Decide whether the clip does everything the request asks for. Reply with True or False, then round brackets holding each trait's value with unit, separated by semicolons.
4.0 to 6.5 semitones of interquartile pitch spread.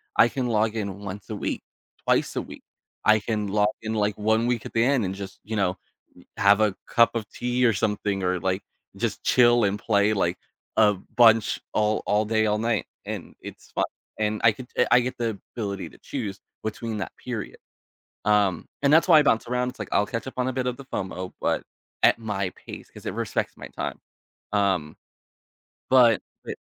False (2.8 semitones)